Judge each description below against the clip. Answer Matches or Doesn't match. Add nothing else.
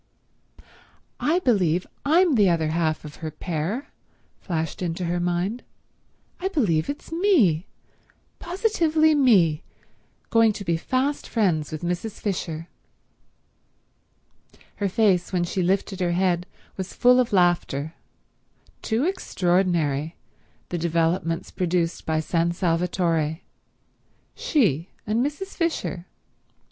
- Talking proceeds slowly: Matches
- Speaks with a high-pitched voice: Doesn't match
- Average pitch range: Doesn't match